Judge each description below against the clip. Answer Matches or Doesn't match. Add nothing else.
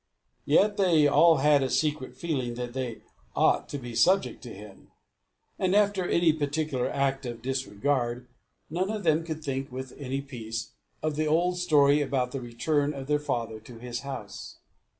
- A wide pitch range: Doesn't match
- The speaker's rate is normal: Matches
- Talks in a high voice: Doesn't match